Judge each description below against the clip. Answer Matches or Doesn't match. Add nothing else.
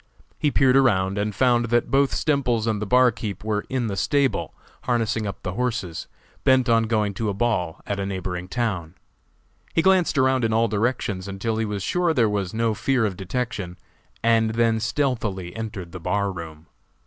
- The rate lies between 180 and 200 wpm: Matches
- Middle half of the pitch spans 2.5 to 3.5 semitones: Doesn't match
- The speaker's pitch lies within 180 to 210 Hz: Doesn't match